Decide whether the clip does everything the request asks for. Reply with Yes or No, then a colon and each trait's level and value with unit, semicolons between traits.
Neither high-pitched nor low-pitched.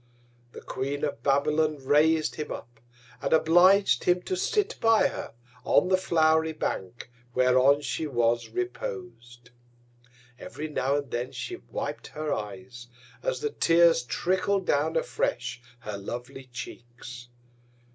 Yes: medium, 150 Hz